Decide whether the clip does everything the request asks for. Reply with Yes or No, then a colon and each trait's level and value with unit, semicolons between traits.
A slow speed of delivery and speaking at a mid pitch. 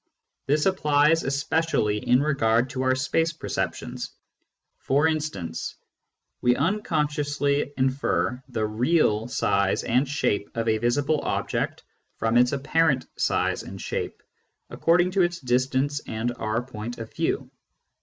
No: slow, 125 wpm; low, 130 Hz